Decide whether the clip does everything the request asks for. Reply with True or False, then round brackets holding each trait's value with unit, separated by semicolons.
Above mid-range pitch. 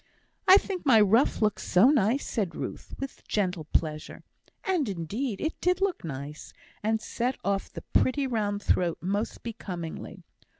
True (215 Hz)